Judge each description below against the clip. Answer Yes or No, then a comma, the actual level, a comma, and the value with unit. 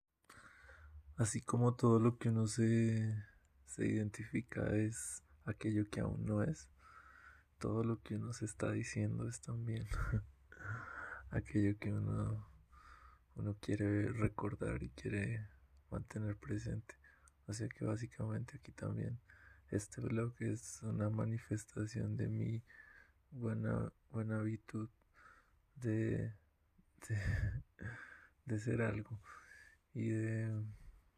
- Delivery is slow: Yes, slow, 110 wpm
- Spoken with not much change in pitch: Yes, narrow, 1.7 semitones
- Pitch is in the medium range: No, low, 110 Hz